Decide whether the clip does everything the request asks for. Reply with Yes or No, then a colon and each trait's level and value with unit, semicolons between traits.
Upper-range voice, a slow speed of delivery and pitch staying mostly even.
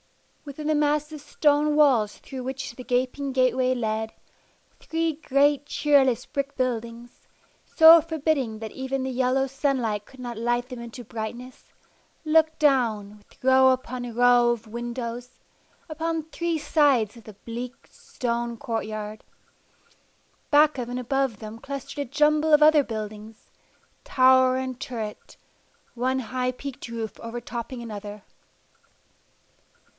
No: very high, 255 Hz; slow, 130 wpm; average, 3.4 semitones